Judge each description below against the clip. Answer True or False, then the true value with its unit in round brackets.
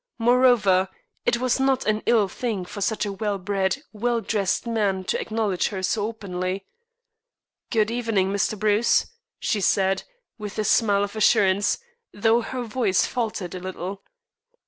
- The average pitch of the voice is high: True (210 Hz)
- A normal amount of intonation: True (3.0 semitones)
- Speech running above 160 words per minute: False (150 wpm)